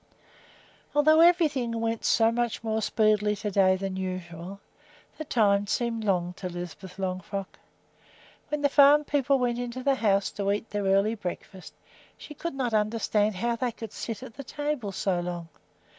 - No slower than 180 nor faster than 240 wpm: No, average, 165 wpm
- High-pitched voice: Yes, high, 215 Hz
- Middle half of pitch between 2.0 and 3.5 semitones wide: No, average, 4.2 semitones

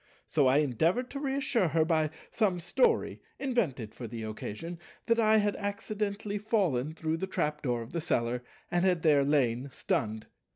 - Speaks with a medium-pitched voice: Yes, medium, 165 Hz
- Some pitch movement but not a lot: No, wide, 8.1 semitones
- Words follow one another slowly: No, average, 170 wpm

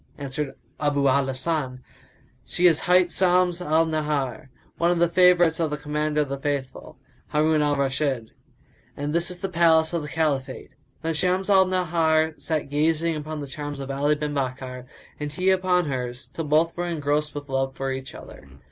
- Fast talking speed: No, average, 185 wpm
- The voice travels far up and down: No, average, 3.3 semitones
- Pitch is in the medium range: Yes, medium, 150 Hz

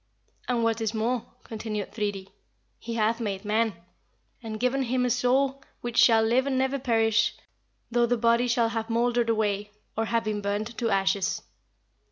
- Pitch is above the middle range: Yes, high, 230 Hz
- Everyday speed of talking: Yes, average, 170 wpm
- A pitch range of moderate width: No, narrow, 2.1 semitones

